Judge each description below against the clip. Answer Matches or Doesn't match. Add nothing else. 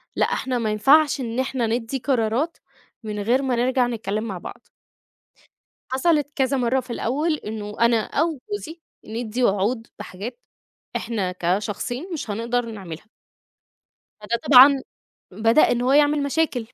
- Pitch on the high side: Matches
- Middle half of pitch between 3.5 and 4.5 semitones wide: Matches